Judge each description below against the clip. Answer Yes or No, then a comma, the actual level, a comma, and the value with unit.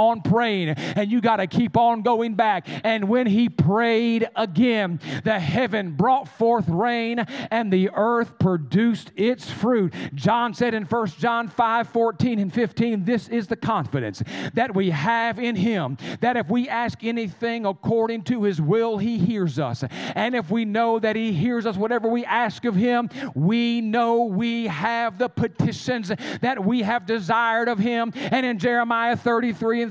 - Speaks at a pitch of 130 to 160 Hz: No, high, 230 Hz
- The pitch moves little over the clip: Yes, narrow, 2.3 semitones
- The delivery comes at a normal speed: Yes, average, 175 wpm